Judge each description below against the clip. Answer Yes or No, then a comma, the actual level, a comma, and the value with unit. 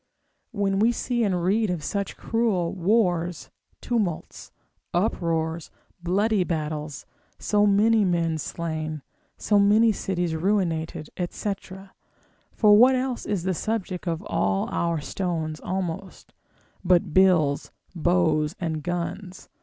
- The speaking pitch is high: No, medium, 180 Hz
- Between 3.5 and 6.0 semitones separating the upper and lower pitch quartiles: Yes, average, 3.9 semitones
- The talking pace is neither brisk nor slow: No, slow, 115 wpm